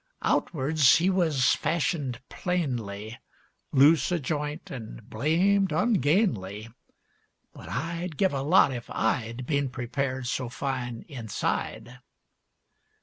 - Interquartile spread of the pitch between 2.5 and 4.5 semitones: No, average, 5.1 semitones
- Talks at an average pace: No, slow, 105 wpm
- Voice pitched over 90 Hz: Yes, medium, 140 Hz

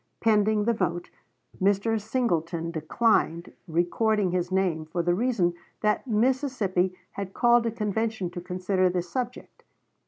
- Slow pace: Yes, slow, 130 wpm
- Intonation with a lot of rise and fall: No, average, 4.2 semitones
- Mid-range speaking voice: No, high, 195 Hz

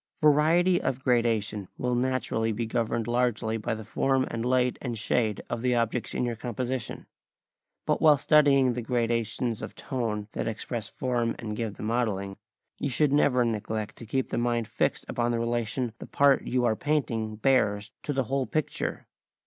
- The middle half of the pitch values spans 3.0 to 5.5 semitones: No, narrow, 2.5 semitones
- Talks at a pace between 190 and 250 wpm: No, average, 180 wpm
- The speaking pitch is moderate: No, low, 120 Hz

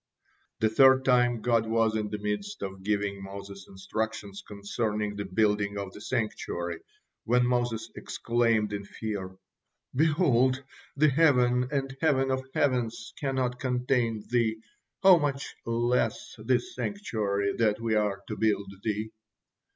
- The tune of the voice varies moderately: Yes, average, 3.7 semitones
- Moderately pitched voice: No, low, 115 Hz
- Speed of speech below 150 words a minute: Yes, slow, 135 wpm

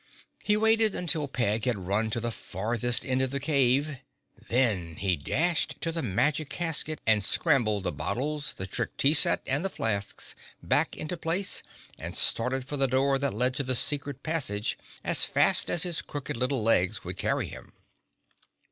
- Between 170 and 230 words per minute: Yes, average, 175 wpm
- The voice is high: No, low, 130 Hz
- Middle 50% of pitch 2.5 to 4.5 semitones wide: No, average, 5.2 semitones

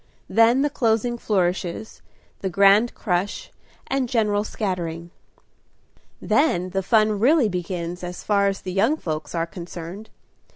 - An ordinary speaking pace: No, slow, 130 wpm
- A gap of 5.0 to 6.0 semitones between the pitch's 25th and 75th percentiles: No, average, 4.0 semitones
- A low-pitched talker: No, high, 200 Hz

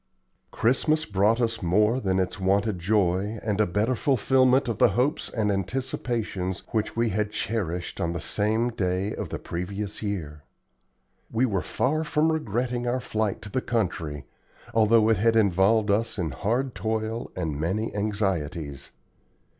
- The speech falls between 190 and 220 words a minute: No, average, 155 wpm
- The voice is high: No, low, 105 Hz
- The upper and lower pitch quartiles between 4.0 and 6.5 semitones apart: No, average, 3.6 semitones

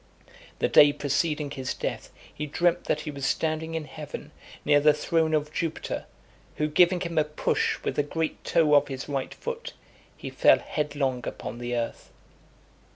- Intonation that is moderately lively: No, narrow, 2.0 semitones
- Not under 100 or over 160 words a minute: No, average, 170 wpm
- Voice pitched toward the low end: No, medium, 150 Hz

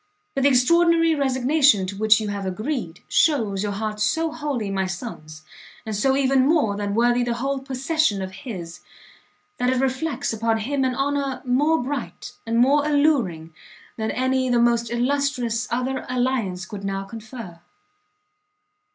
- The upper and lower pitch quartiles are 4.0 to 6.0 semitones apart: Yes, average, 4.7 semitones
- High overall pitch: Yes, high, 245 Hz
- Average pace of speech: Yes, average, 155 wpm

